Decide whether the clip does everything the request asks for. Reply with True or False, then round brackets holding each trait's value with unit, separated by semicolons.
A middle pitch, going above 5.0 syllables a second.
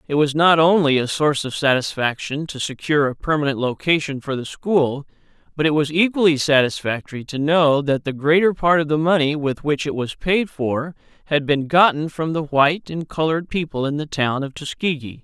True (150 Hz; 5.3 syllables/s)